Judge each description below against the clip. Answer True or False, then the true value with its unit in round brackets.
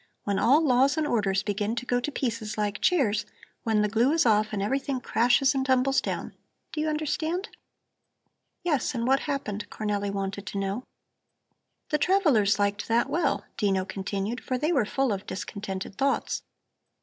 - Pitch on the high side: True (235 Hz)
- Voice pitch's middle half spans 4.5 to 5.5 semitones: True (5.1 semitones)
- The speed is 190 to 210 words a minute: False (170 wpm)